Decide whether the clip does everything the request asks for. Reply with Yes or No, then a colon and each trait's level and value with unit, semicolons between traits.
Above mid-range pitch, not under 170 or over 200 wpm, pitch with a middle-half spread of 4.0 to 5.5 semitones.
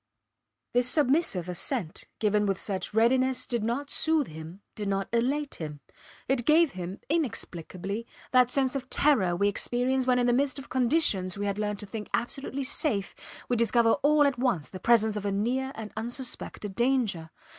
Yes: high, 235 Hz; average, 175 wpm; average, 4.7 semitones